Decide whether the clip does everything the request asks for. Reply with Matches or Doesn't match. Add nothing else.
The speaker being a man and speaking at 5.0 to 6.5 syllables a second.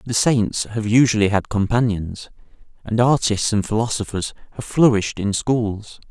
Doesn't match